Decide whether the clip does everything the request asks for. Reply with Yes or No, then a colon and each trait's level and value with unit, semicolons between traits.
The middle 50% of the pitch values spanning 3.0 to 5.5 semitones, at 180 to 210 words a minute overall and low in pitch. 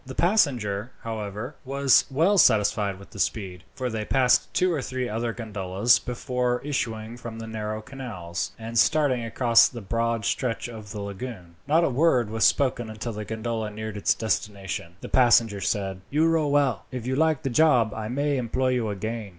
Yes: average, 3.5 semitones; average, 185 wpm; low, 115 Hz